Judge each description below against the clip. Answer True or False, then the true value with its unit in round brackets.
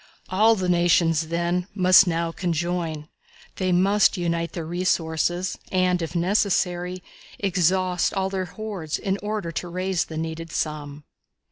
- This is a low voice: False (175 Hz)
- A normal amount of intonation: False (2.0 semitones)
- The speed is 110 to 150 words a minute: True (135 wpm)